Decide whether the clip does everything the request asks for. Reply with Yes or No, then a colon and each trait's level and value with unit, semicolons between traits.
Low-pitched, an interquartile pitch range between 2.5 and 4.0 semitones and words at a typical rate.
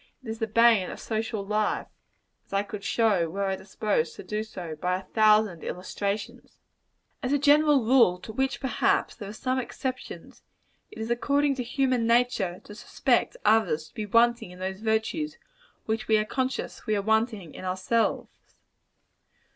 No: high, 220 Hz; average, 3.5 semitones; average, 170 wpm